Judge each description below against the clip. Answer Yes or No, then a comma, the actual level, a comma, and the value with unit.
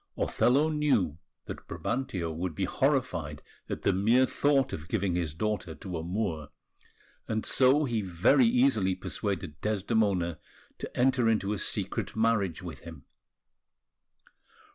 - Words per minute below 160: Yes, slow, 135 wpm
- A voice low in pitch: Yes, low, 105 Hz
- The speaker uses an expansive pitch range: Yes, wide, 6.3 semitones